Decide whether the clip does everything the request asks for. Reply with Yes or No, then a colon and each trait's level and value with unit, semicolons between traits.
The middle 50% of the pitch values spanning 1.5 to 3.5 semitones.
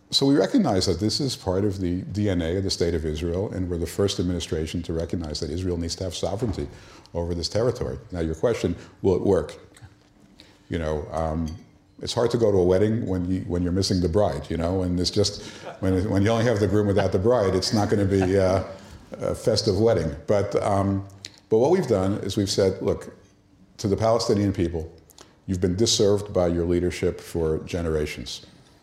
Yes: average, 2.8 semitones